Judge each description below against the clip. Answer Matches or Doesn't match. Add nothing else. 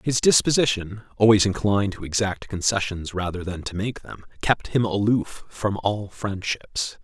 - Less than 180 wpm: Matches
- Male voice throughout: Matches